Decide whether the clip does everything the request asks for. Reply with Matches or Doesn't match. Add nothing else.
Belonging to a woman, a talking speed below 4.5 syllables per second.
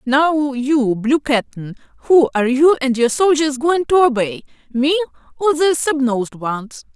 Matches